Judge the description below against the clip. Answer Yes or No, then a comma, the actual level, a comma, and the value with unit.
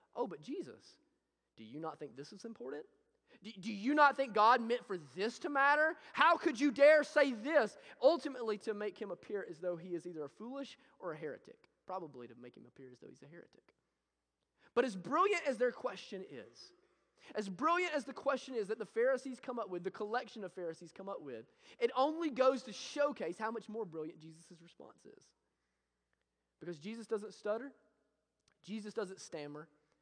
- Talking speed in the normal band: Yes, average, 195 wpm